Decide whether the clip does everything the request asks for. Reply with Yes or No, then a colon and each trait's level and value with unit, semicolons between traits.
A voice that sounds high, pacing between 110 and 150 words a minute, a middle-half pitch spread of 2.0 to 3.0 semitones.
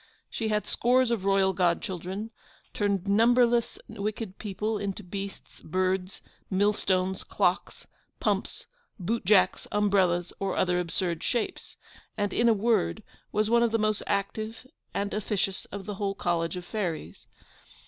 Yes: high, 200 Hz; average, 140 wpm; narrow, 2.6 semitones